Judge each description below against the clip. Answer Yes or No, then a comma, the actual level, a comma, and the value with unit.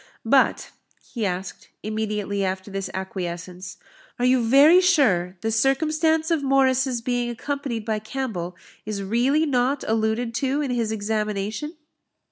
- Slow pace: Yes, slow, 130 wpm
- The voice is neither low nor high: No, high, 230 Hz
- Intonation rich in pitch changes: No, average, 5.0 semitones